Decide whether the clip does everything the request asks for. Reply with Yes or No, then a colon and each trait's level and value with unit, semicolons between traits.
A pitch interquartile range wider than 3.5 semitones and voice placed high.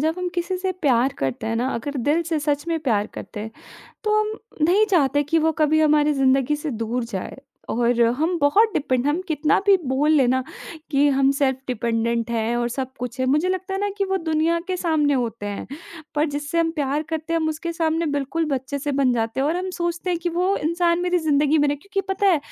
Yes: average, 4.6 semitones; very high, 295 Hz